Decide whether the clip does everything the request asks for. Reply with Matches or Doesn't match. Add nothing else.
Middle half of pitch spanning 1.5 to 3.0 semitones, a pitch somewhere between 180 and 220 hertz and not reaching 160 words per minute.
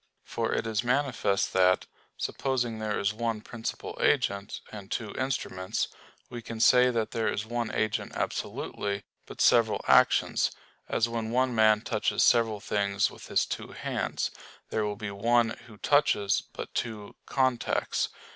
Doesn't match